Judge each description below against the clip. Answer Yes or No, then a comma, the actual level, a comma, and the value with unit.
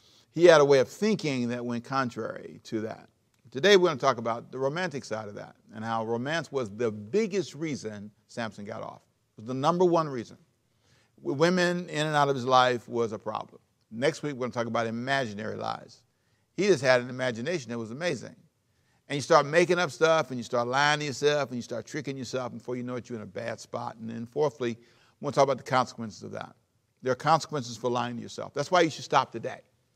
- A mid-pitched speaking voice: No, low, 125 Hz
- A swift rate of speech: Yes, fast, 230 wpm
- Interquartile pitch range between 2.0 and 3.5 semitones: No, average, 4.1 semitones